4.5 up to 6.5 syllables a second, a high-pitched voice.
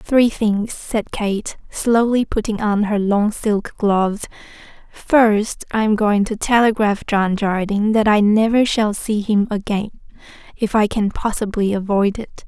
No: 4.0 syllables/s; high, 210 Hz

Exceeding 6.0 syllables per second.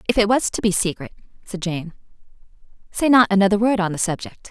Yes: 6.3 syllables/s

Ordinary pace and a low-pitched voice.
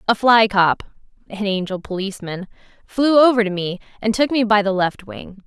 No: average, 165 wpm; high, 210 Hz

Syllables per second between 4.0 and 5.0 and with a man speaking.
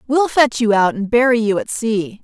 No: 4.8 syllables/s; female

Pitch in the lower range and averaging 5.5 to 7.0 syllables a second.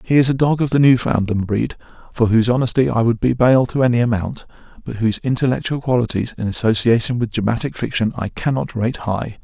Yes: low, 120 Hz; 6.0 syllables/s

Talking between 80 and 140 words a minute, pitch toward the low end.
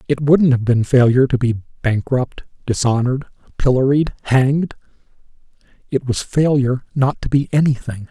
Yes: slow, 135 wpm; low, 130 Hz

